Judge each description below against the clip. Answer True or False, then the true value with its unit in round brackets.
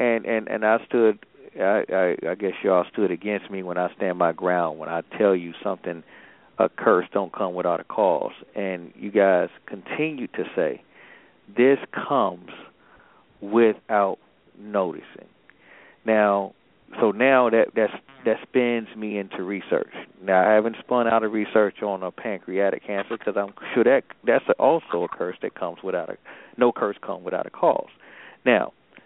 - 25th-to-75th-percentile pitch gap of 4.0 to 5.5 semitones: False (2.7 semitones)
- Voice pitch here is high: False (105 Hz)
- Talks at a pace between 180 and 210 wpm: False (165 wpm)